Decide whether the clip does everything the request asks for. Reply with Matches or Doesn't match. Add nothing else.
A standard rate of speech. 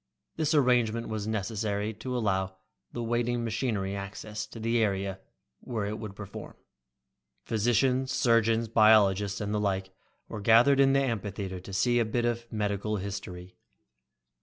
Matches